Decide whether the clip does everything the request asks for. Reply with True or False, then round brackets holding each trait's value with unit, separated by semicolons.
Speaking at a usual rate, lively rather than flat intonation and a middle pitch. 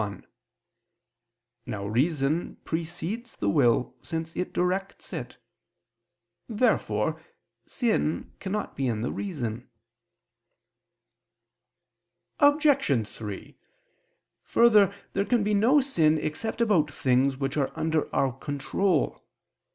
False (95 wpm; 7.6 semitones; 160 Hz)